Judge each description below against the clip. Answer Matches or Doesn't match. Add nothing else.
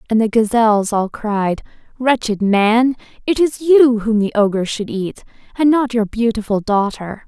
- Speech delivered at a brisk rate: Doesn't match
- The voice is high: Matches